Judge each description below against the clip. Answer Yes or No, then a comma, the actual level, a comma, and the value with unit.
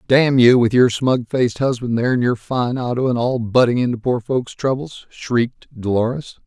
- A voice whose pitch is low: Yes, low, 125 Hz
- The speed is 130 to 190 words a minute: No, fast, 205 wpm